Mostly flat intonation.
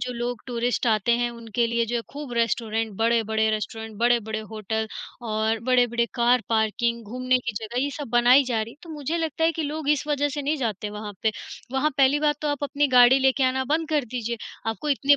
No: average, 3.7 semitones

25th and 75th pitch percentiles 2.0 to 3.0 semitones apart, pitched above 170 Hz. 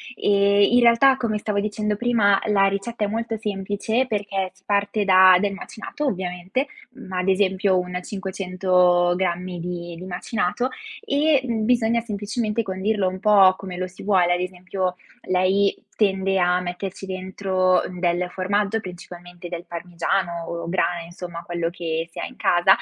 Yes: narrow, 2.6 semitones; high, 190 Hz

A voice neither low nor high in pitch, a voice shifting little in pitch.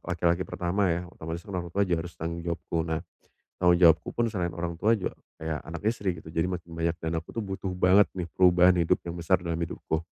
No: very low, 85 Hz; narrow, 1.8 semitones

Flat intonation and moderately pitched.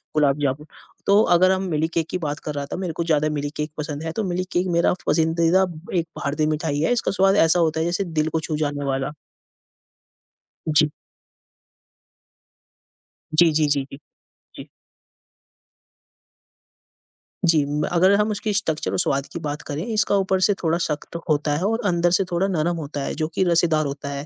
No: average, 3.0 semitones; medium, 160 Hz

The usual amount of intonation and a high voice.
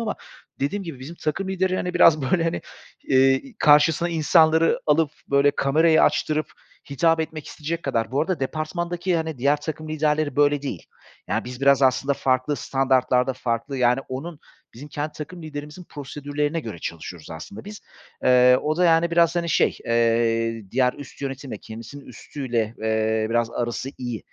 No: average, 4.2 semitones; medium, 145 Hz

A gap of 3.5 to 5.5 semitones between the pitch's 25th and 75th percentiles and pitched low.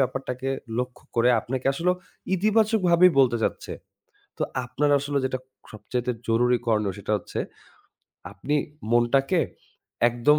Yes: average, 3.8 semitones; low, 130 Hz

